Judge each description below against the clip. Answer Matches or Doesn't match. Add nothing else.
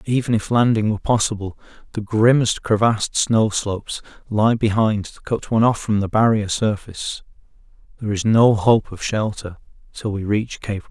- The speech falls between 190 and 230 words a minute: Doesn't match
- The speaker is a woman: Doesn't match